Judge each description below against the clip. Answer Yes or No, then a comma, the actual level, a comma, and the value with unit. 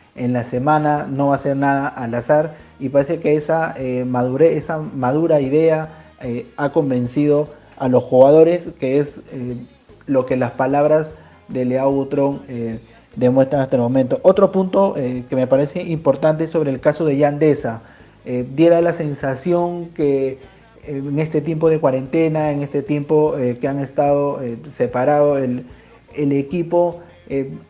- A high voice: No, medium, 140 Hz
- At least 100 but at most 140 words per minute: No, average, 165 wpm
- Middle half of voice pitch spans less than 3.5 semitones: Yes, average, 3.1 semitones